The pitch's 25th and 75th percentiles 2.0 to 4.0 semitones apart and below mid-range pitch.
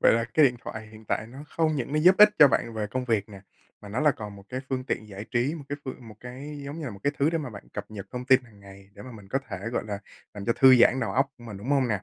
No: average, 4.7 semitones; low, 120 Hz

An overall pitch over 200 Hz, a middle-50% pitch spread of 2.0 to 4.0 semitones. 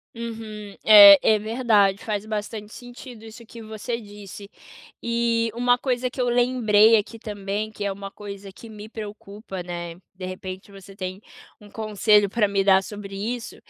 Yes: high, 210 Hz; narrow, 2.4 semitones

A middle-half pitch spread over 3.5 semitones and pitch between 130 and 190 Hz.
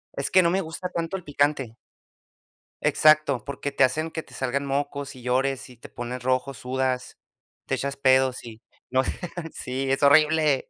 No: average, 3.0 semitones; medium, 140 Hz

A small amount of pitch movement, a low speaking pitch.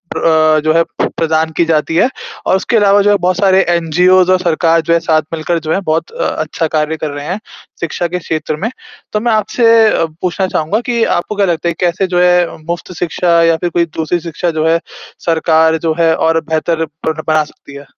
No: narrow, 2.3 semitones; medium, 170 Hz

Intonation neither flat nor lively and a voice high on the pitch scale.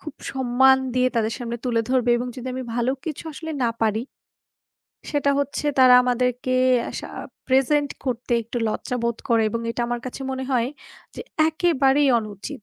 No: narrow, 2.2 semitones; very high, 250 Hz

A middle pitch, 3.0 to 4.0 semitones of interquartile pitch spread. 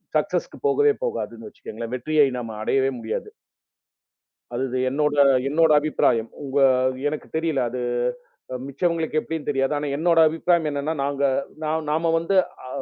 Yes: medium, 150 Hz; average, 3.4 semitones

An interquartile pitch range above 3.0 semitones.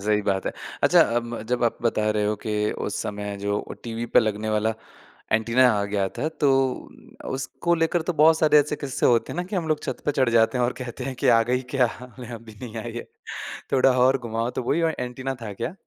Yes: average, 3.7 semitones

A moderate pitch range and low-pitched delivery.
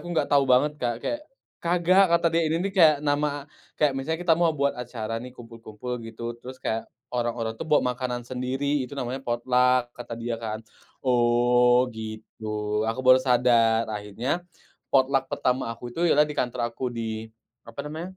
Yes: average, 3.6 semitones; low, 125 Hz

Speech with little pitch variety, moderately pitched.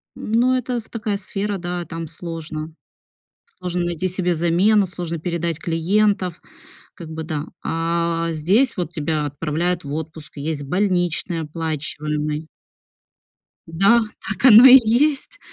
No: average, 3.8 semitones; medium, 170 Hz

